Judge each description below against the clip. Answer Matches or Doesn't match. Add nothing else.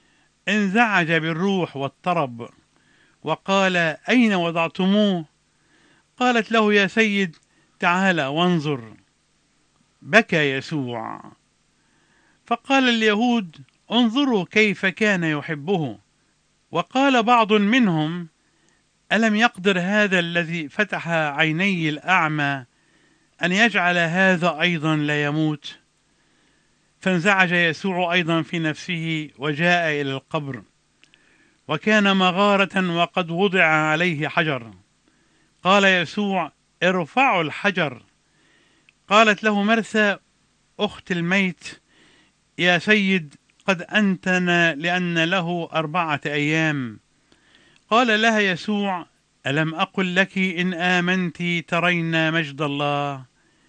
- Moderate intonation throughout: Matches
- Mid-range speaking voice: Matches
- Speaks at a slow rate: Matches